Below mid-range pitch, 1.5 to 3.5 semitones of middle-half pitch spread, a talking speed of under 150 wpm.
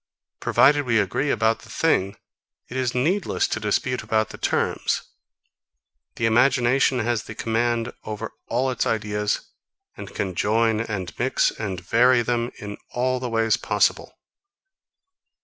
Yes: low, 115 Hz; average, 2.8 semitones; average, 140 wpm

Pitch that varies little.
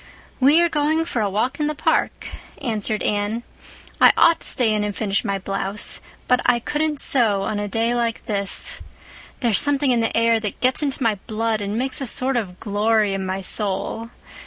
No: average, 4.1 semitones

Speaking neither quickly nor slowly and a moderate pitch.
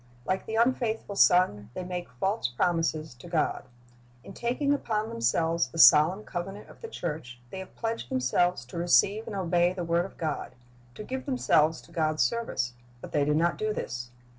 Yes: average, 190 wpm; medium, 175 Hz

